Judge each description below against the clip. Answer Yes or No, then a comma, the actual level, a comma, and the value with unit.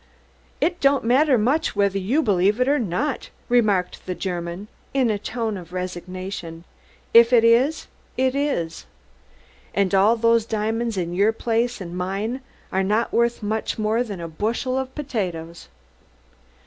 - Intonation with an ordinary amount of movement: Yes, average, 4.7 semitones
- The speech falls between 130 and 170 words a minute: Yes, average, 150 wpm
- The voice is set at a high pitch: Yes, high, 215 Hz